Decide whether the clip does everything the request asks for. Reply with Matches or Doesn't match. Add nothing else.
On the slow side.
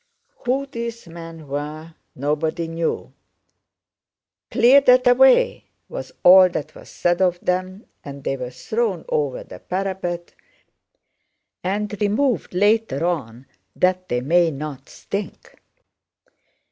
Matches